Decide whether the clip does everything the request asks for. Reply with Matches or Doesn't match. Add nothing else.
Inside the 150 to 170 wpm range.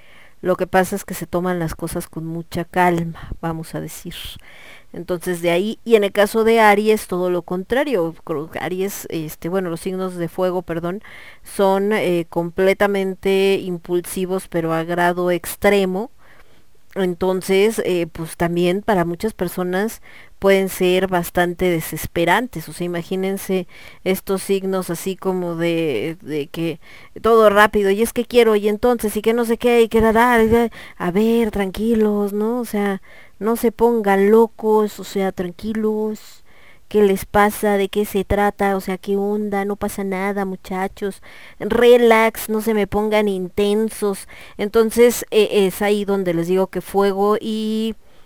Matches